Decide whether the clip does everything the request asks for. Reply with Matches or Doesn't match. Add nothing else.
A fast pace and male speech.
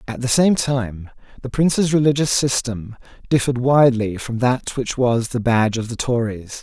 Doesn't match